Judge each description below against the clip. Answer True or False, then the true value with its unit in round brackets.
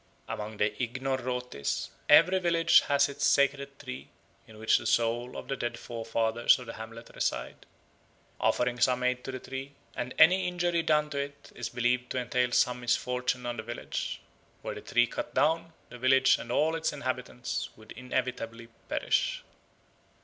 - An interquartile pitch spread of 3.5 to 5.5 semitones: False (2.9 semitones)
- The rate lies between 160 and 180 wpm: True (165 wpm)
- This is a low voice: True (125 Hz)